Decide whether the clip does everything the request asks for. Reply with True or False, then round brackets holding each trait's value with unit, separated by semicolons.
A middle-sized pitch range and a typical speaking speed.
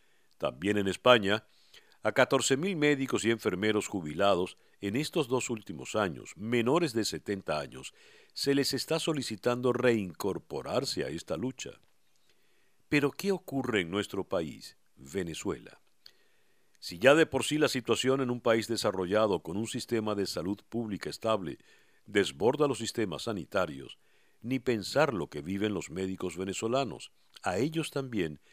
True (4.8 semitones; 140 wpm)